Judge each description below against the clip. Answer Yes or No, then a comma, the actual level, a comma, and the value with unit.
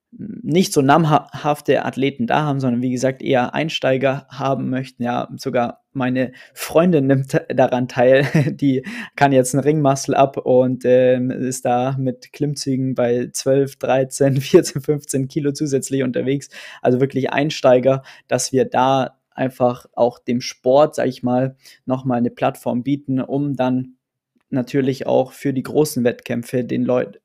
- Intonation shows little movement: Yes, narrow, 1.8 semitones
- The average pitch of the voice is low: Yes, low, 130 Hz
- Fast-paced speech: No, average, 150 wpm